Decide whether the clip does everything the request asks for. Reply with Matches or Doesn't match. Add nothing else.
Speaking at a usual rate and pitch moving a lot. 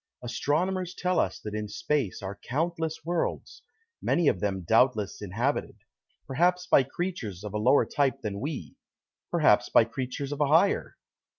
Matches